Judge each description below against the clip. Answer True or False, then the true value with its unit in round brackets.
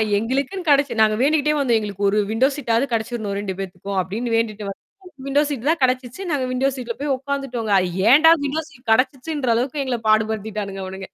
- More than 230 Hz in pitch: True (245 Hz)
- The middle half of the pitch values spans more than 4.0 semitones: True (4.4 semitones)